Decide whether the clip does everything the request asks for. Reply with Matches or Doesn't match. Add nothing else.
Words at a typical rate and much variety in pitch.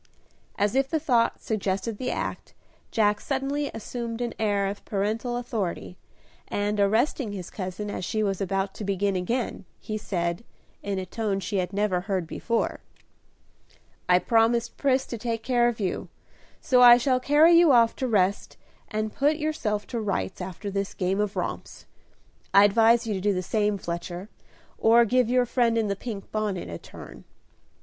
Doesn't match